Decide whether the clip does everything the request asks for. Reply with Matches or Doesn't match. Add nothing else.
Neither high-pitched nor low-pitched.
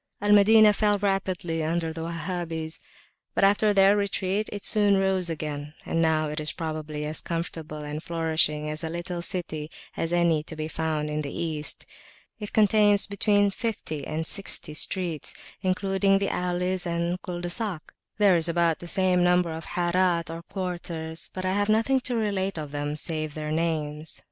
Matches